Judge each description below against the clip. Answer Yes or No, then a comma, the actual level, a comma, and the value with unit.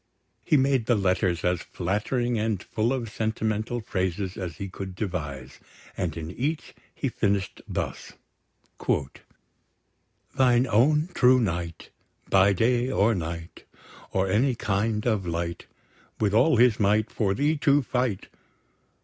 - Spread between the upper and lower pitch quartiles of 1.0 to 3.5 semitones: No, average, 4.8 semitones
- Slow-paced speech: Yes, slow, 130 wpm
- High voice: No, low, 105 Hz